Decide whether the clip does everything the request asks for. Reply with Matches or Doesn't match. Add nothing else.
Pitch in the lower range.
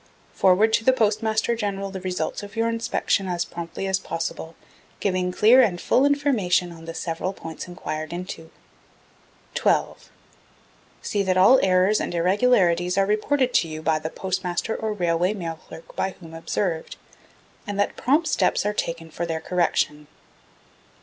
Doesn't match